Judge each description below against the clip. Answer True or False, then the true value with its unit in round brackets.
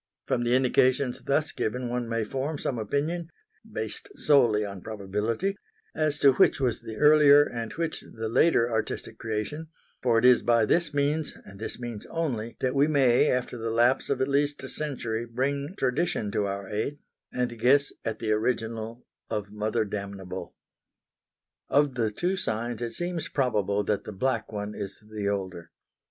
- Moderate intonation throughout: True (4.7 semitones)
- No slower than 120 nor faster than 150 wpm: False (170 wpm)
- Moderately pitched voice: False (120 Hz)